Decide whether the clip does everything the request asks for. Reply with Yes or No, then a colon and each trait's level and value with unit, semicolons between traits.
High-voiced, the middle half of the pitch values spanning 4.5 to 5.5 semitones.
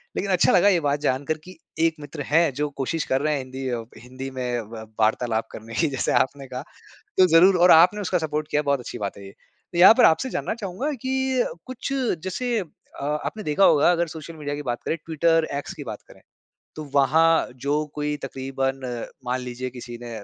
No: medium, 150 Hz; average, 5.0 semitones